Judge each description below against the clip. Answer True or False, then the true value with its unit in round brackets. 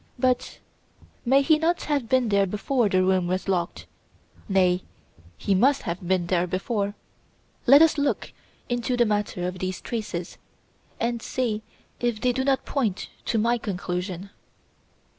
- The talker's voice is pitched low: False (210 Hz)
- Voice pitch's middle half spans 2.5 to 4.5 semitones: False (5.2 semitones)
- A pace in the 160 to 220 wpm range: False (150 wpm)